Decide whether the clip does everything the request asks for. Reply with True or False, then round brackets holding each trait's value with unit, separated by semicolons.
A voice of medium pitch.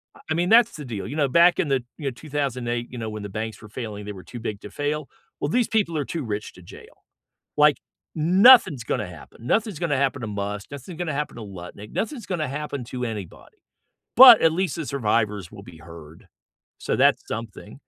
False (130 Hz)